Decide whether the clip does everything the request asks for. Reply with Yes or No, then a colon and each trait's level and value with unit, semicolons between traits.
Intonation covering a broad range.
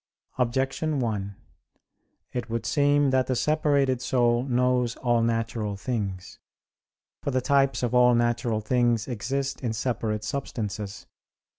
No: average, 2.7 semitones